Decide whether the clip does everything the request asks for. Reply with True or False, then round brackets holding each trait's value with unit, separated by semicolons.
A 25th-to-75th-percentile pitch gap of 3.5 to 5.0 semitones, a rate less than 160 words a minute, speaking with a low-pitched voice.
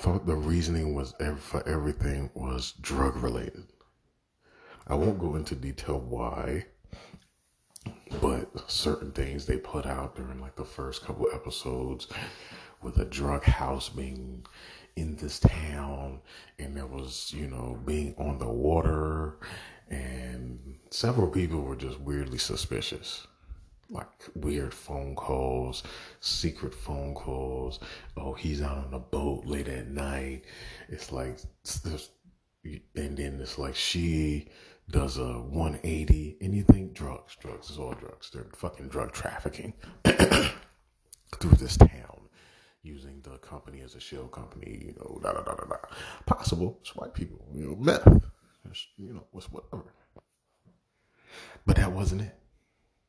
False (2.9 semitones; 140 wpm; 70 Hz)